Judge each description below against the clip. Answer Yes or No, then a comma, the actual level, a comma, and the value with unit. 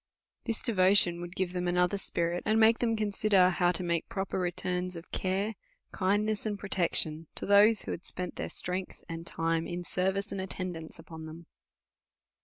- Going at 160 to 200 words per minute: Yes, average, 180 wpm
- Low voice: No, medium, 185 Hz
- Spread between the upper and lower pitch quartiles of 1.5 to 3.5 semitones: Yes, narrow, 2.6 semitones